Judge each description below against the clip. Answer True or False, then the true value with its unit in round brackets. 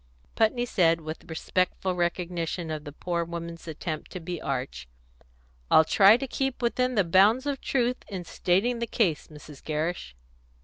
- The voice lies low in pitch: False (175 Hz)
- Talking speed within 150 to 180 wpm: True (160 wpm)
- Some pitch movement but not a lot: False (5.7 semitones)